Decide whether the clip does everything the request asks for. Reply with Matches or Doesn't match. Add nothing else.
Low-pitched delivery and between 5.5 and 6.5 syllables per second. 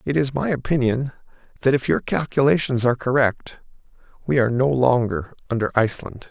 Matches